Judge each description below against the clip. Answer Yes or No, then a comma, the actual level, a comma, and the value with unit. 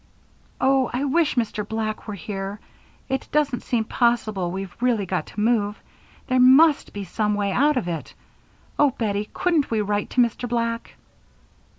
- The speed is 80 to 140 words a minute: No, average, 165 wpm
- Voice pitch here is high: Yes, high, 230 Hz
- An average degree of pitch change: Yes, average, 3.8 semitones